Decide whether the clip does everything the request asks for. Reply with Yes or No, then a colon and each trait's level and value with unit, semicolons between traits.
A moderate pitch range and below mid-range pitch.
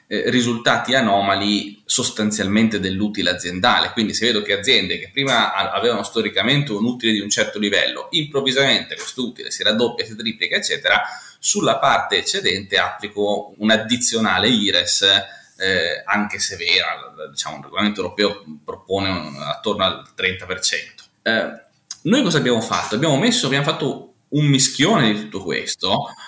Yes: average, 3.6 semitones; low, 110 Hz